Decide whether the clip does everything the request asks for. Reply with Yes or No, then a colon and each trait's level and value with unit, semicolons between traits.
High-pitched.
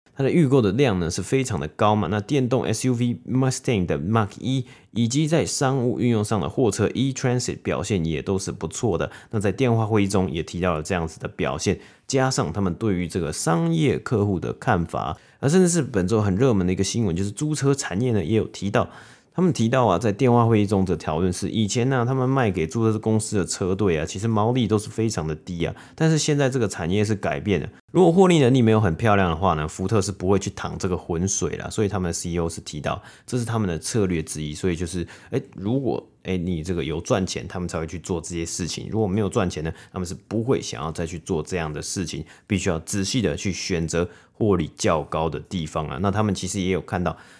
No: low, 100 Hz